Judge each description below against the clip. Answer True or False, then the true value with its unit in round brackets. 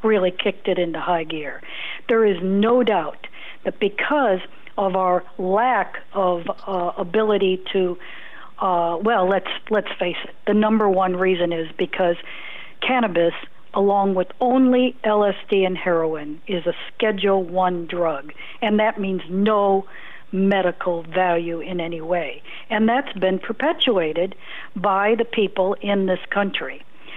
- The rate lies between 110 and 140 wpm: True (135 wpm)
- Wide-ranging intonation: False (2.7 semitones)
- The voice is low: False (190 Hz)